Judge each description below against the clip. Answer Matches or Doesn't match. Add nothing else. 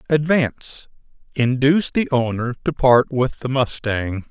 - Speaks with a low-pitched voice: Matches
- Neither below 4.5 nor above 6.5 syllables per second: Doesn't match